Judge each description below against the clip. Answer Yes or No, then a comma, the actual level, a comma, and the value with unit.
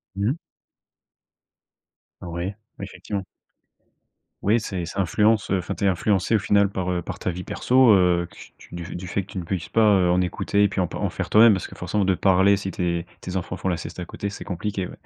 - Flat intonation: Yes, narrow, 2.3 semitones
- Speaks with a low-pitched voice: Yes, very low, 95 Hz